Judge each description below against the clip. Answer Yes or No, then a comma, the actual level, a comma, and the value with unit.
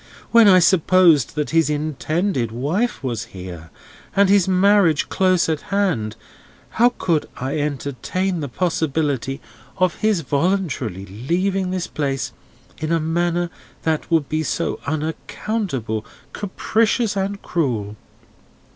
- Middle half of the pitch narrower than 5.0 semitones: No, average, 5.3 semitones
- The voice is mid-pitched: Yes, medium, 165 Hz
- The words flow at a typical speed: No, slow, 120 wpm